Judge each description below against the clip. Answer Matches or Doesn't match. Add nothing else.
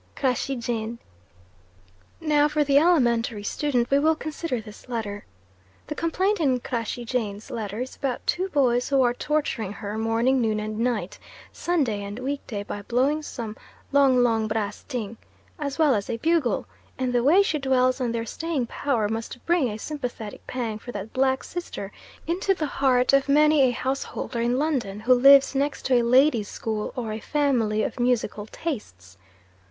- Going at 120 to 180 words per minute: Matches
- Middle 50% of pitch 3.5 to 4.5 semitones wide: Matches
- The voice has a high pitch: Matches